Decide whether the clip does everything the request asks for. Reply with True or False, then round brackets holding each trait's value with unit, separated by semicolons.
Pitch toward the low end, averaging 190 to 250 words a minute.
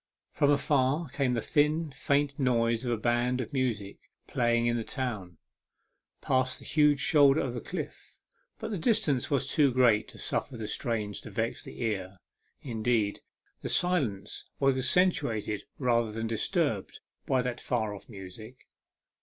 False (125 Hz; 155 wpm)